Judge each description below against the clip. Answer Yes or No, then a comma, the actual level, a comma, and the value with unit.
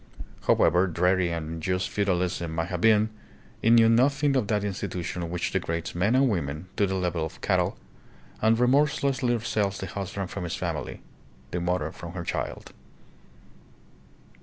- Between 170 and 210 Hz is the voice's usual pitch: No, very low, 95 Hz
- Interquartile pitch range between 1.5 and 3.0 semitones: No, average, 4.4 semitones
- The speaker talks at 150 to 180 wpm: Yes, average, 160 wpm